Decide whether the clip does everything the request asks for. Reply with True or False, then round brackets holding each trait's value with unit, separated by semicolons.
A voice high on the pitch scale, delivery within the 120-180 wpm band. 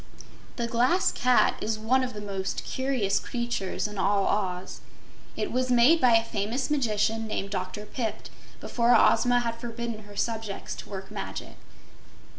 True (225 Hz; 155 wpm)